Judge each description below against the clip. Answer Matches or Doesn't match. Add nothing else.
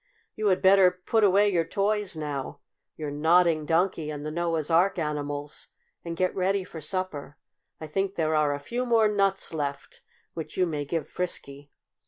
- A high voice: Doesn't match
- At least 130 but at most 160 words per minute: Doesn't match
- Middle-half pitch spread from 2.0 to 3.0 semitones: Doesn't match